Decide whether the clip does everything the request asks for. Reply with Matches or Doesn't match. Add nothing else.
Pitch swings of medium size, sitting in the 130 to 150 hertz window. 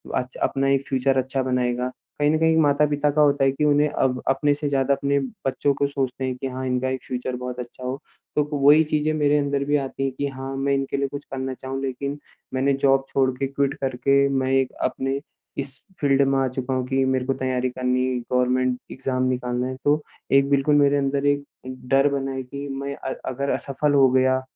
Doesn't match